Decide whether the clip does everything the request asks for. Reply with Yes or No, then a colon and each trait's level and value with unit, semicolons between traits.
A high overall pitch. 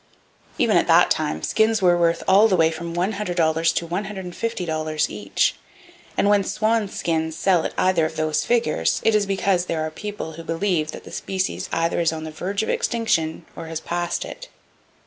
No: medium, 175 Hz